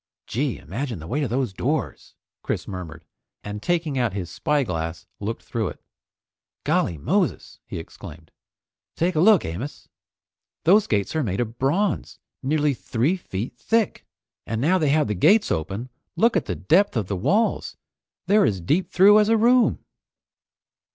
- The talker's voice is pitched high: No, low, 130 Hz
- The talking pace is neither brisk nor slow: Yes, average, 160 wpm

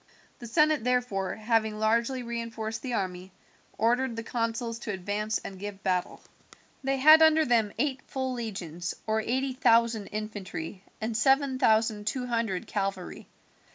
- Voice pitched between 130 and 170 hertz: No, high, 225 Hz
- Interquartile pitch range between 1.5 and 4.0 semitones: Yes, average, 3.2 semitones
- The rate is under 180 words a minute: Yes, average, 145 wpm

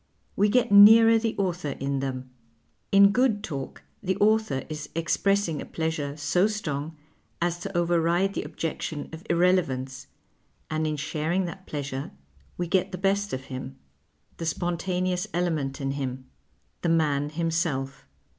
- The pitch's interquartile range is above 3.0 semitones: Yes, average, 5.1 semitones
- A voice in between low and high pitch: Yes, medium, 170 Hz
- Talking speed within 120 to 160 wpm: Yes, average, 145 wpm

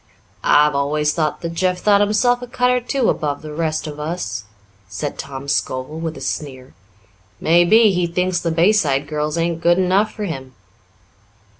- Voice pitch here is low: No, medium, 165 Hz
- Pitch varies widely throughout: No, average, 4.1 semitones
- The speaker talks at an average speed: Yes, average, 170 wpm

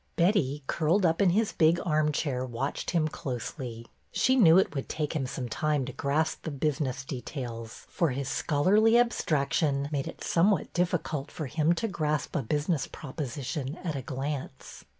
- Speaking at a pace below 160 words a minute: No, average, 170 wpm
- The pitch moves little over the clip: No, average, 3.9 semitones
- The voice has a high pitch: No, medium, 150 Hz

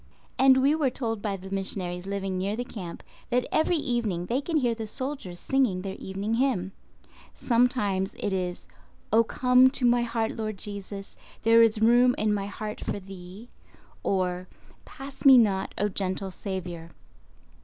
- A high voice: Yes, high, 210 Hz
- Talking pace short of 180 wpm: Yes, average, 160 wpm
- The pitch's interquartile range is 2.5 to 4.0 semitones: No, average, 4.4 semitones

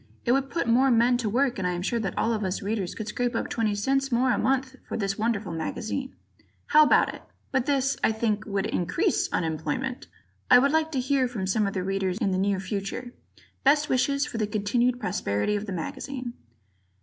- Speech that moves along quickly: Yes, fast, 215 wpm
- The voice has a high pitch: Yes, high, 230 Hz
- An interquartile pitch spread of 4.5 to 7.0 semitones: Yes, average, 5.0 semitones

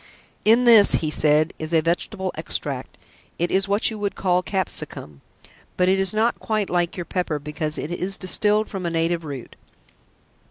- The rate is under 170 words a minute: No, average, 175 wpm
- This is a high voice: No, medium, 180 Hz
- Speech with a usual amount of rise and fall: Yes, average, 3.9 semitones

